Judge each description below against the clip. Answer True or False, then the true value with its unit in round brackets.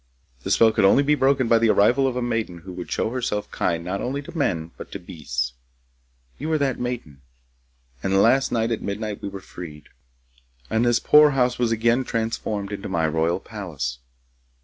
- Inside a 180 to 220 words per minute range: True (195 wpm)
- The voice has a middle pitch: False (110 Hz)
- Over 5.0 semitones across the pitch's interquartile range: True (5.6 semitones)